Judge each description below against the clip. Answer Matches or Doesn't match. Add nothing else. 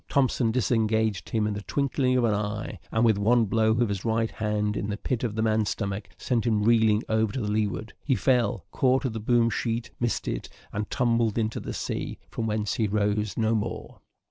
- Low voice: Matches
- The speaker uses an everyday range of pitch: Doesn't match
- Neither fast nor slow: Doesn't match